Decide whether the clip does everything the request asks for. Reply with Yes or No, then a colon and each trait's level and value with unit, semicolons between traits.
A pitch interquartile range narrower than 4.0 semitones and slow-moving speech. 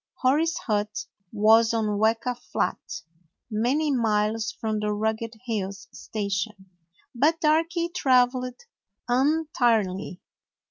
Yes: average, 3.5 semitones; slow, 95 wpm